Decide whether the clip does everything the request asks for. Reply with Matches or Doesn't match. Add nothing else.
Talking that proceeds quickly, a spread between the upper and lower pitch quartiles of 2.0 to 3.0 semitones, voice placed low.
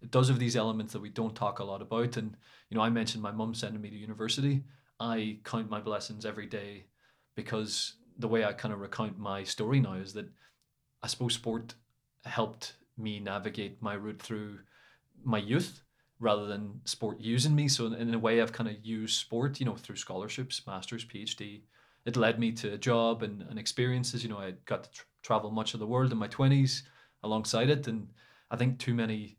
Matches